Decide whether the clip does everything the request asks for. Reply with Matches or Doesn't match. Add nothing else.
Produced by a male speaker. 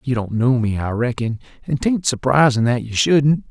Matches